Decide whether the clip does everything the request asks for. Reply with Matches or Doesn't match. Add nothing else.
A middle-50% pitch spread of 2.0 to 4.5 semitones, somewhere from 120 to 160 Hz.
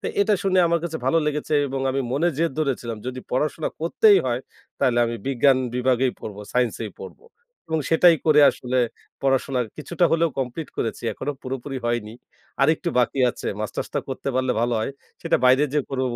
Matches